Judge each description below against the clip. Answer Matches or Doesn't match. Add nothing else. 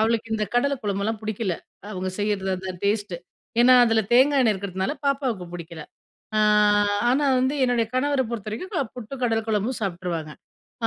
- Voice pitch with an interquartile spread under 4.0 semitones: Doesn't match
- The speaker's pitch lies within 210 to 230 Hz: Matches